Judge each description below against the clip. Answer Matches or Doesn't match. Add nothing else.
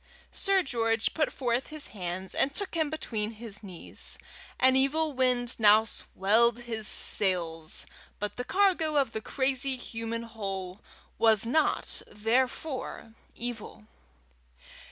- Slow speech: Matches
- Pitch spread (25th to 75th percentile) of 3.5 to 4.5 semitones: Matches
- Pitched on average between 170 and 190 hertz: Doesn't match